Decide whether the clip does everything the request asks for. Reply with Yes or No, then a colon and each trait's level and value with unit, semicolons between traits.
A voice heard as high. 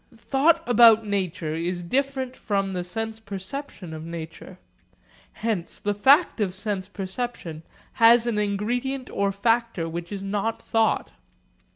Yes: high, 205 Hz